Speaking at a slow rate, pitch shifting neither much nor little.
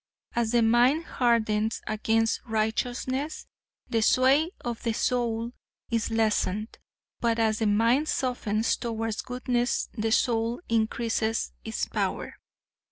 No: slow, 115 wpm; narrow, 1.8 semitones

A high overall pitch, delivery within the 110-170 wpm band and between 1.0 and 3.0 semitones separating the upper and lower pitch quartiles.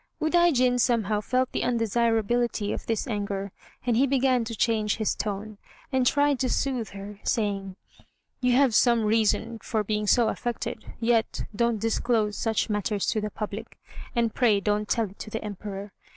Yes: high, 225 Hz; average, 165 wpm; narrow, 2.6 semitones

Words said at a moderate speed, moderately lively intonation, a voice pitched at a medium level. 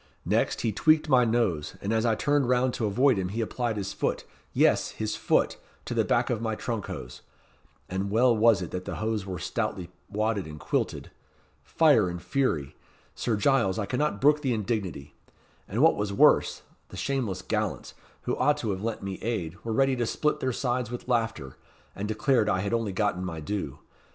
No: average, 195 wpm; average, 4.2 semitones; low, 110 Hz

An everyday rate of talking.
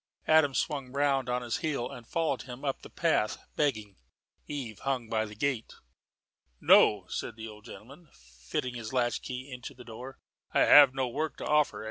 Yes: average, 175 wpm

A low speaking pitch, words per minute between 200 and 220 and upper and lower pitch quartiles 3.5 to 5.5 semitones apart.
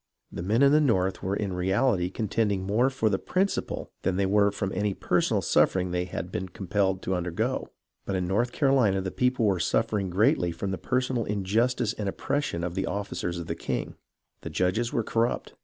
Yes: low, 100 Hz; fast, 205 wpm; average, 3.8 semitones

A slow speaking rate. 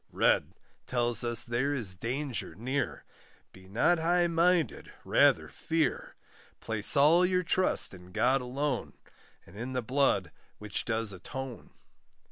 Yes: slow, 130 wpm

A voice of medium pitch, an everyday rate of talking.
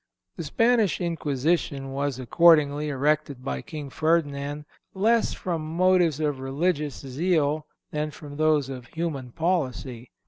No: medium, 150 Hz; slow, 125 wpm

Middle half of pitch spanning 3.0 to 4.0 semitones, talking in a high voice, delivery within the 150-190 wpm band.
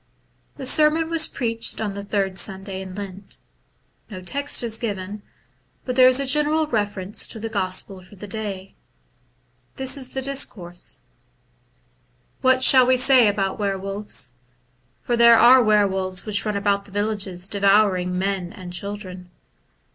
No: average, 4.4 semitones; high, 205 Hz; average, 155 wpm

